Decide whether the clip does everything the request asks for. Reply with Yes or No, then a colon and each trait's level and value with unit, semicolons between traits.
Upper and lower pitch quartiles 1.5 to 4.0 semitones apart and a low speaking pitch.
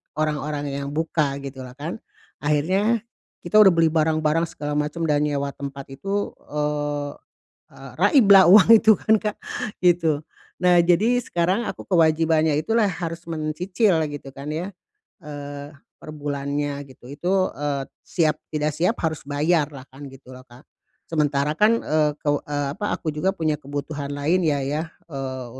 No: average, 3.3 semitones; medium, 150 Hz